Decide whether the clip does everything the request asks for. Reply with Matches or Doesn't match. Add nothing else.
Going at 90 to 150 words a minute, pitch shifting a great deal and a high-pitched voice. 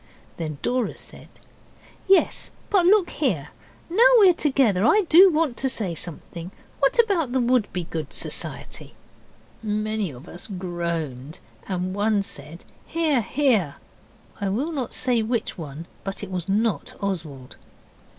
Matches